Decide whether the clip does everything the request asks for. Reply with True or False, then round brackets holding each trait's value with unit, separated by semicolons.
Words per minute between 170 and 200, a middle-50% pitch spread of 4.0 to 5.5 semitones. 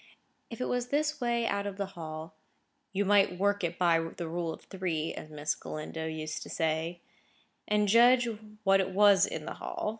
True (190 wpm; 4.3 semitones)